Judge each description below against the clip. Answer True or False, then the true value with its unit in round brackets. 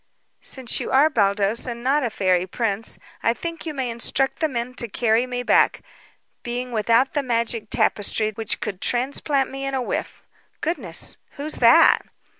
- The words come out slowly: False (170 wpm)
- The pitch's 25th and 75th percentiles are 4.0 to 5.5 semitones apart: False (3.5 semitones)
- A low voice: False (240 Hz)